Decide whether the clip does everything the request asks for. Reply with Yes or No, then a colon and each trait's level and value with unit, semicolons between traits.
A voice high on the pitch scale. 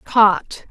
Yes: high, 195 Hz